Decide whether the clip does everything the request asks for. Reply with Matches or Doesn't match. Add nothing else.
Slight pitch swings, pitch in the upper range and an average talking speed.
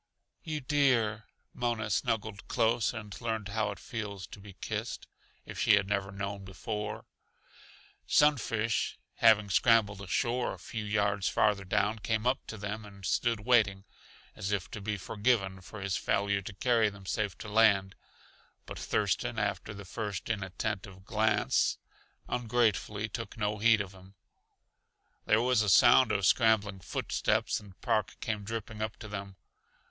Doesn't match